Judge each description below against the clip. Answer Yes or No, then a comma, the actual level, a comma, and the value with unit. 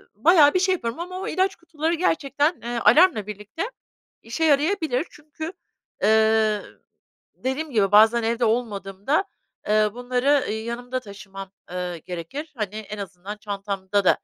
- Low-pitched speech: No, high, 235 Hz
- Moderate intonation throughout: No, wide, 6.8 semitones